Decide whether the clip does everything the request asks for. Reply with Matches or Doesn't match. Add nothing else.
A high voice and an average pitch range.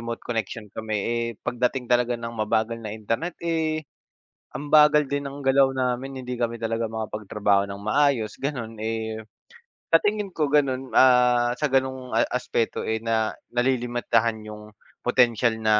Doesn't match